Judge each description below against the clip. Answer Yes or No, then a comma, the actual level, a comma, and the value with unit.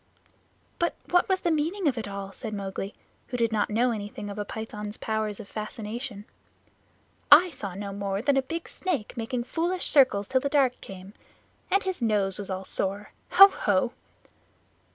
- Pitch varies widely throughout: Yes, wide, 5.7 semitones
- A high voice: Yes, high, 220 Hz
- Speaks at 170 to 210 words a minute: Yes, average, 175 wpm